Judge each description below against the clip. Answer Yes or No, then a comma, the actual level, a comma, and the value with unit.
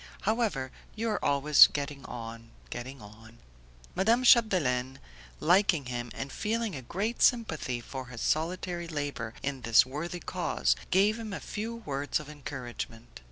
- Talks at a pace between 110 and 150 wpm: Yes, average, 145 wpm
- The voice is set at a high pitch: No, medium, 145 Hz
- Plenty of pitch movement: Yes, wide, 8.1 semitones